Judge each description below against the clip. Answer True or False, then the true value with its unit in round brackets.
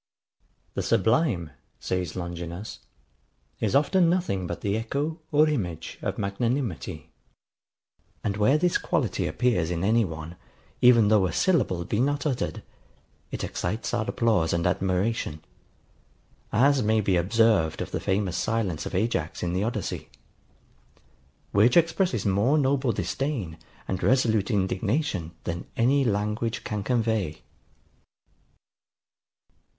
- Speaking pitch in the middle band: False (105 Hz)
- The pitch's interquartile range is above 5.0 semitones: True (5.5 semitones)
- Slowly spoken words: True (125 wpm)